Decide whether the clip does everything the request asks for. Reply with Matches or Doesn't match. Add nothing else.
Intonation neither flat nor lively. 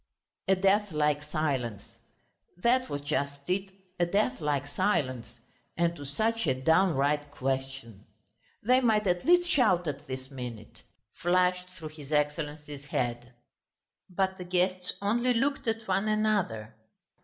Doesn't match